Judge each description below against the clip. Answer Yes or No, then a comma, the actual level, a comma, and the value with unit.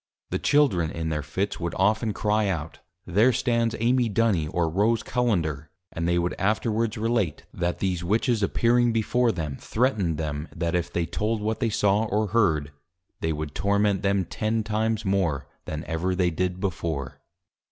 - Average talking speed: Yes, average, 175 wpm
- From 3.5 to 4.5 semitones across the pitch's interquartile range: No, average, 5.0 semitones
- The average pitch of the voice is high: No, low, 100 Hz